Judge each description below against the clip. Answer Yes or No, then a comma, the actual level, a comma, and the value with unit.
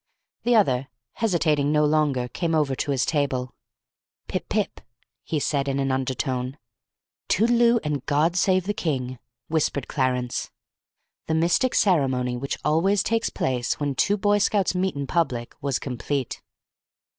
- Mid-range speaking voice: Yes, medium, 145 Hz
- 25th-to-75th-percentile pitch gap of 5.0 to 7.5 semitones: Yes, average, 5.3 semitones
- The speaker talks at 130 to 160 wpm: Yes, average, 145 wpm